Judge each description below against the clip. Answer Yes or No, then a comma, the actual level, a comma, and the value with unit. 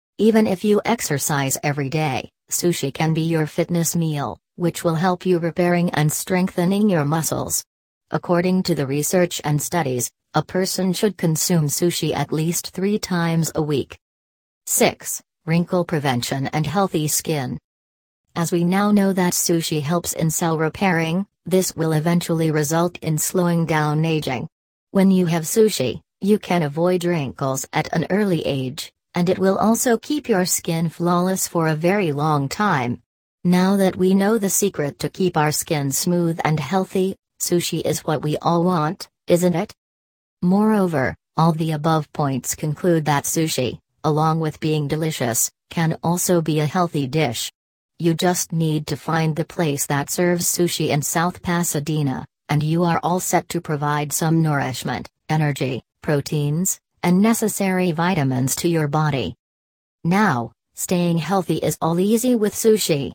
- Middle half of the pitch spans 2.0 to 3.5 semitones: Yes, average, 3.1 semitones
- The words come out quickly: No, average, 155 wpm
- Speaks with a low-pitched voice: No, medium, 165 Hz